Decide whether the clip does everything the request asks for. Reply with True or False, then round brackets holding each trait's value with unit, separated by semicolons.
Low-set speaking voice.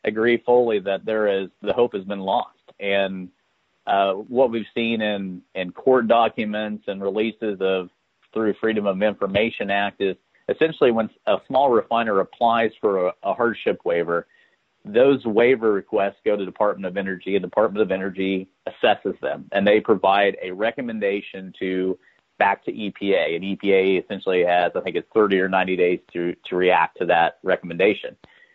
True (100 Hz)